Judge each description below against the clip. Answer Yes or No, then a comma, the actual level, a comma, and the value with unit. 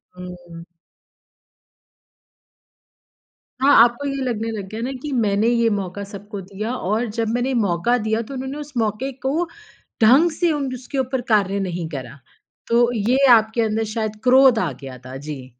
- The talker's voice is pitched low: No, high, 225 Hz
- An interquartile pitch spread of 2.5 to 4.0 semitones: No, average, 4.6 semitones